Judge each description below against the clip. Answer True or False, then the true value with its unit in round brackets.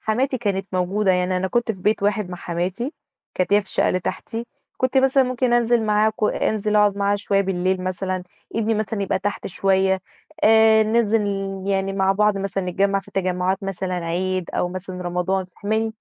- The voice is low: False (195 Hz)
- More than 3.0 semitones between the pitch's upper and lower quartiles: False (2.7 semitones)